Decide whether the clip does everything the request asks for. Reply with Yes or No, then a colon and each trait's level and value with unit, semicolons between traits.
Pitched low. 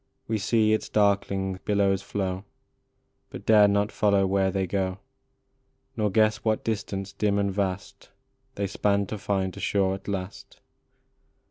Yes: low, 100 Hz